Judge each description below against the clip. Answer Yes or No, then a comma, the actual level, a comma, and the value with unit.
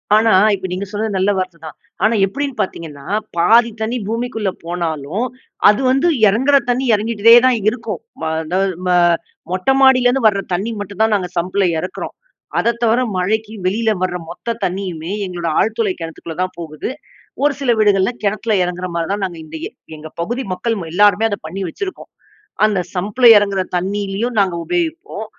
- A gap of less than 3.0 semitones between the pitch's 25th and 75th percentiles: No, average, 4.1 semitones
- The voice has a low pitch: No, high, 205 Hz